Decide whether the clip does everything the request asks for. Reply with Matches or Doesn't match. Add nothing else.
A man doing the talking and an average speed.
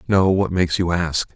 Doesn't match